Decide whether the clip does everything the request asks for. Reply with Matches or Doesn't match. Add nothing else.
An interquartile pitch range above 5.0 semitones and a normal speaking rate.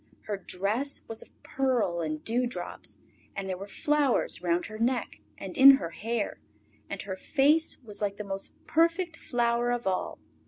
Matches